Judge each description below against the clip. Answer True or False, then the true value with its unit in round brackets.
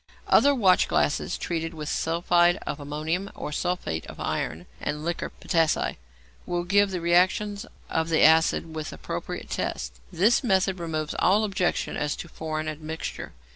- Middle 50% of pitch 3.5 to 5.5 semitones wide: False (3.1 semitones)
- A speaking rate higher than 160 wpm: False (145 wpm)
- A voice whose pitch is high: False (165 Hz)